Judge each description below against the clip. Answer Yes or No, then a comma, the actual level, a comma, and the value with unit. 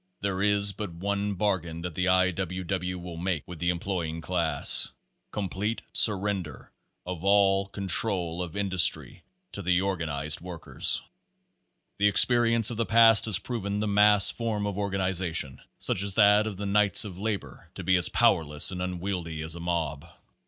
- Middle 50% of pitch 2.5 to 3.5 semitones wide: Yes, average, 2.9 semitones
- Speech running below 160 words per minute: No, average, 165 wpm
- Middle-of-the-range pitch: No, very low, 95 Hz